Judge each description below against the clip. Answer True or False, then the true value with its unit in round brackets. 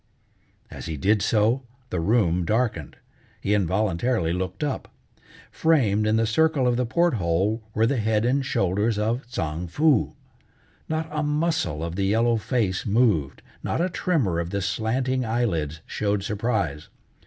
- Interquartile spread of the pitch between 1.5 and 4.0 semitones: False (5.2 semitones)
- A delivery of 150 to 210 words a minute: True (155 wpm)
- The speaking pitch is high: False (110 Hz)